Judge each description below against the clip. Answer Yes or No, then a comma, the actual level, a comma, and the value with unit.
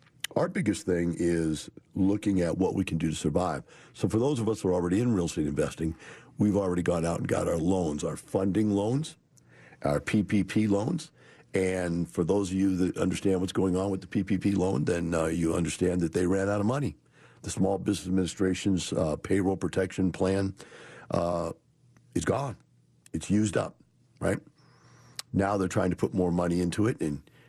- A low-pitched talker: Yes, very low, 95 Hz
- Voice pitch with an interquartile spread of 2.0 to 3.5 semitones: Yes, average, 2.7 semitones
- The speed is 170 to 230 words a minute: Yes, average, 190 wpm